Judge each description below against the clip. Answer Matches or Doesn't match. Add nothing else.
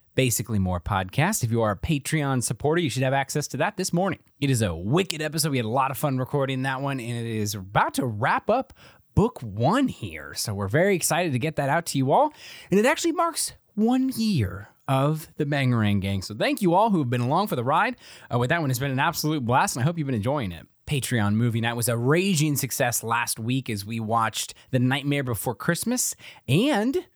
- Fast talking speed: Matches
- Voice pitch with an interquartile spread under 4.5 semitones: Doesn't match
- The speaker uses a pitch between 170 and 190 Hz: Doesn't match